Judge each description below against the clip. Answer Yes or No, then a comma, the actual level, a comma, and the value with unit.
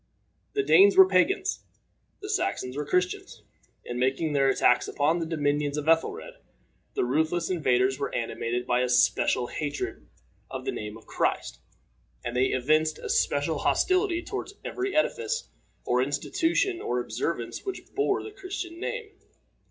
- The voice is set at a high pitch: No, medium, 155 Hz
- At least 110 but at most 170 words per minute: Yes, average, 150 wpm